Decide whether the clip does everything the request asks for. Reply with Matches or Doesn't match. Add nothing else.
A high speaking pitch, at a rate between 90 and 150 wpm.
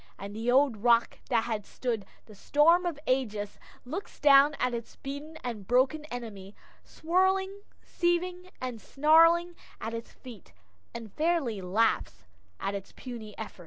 Matches